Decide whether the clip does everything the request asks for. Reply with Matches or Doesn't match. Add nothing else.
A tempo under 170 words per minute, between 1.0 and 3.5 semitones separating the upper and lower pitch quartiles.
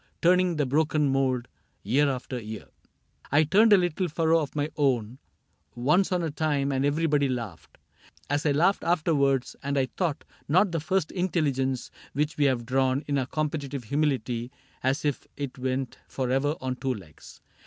Doesn't match